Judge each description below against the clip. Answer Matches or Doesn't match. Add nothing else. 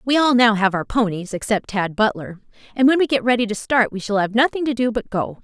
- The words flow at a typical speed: Doesn't match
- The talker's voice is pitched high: Matches